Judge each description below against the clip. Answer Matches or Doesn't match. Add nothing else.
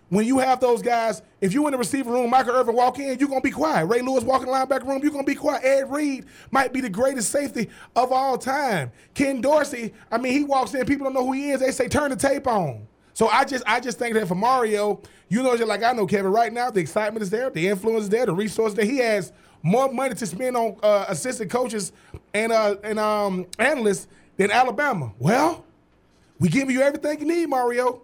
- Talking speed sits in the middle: Doesn't match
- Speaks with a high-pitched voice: Matches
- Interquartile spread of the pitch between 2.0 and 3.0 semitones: Doesn't match